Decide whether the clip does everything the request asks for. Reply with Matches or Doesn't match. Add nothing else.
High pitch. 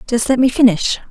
Matches